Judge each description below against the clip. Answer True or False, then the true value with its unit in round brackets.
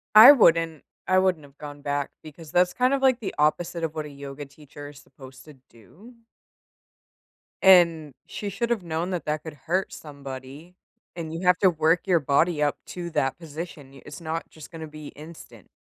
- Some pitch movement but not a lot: True (3.5 semitones)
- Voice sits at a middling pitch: True (160 Hz)